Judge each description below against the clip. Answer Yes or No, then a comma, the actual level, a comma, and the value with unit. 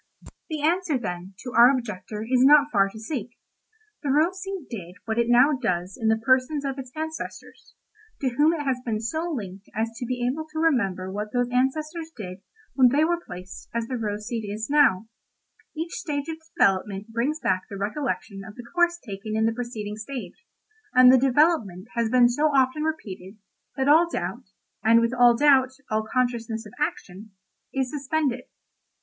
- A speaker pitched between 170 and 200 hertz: No, high, 245 Hz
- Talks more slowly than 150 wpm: No, average, 180 wpm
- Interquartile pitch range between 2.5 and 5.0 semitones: No, wide, 5.4 semitones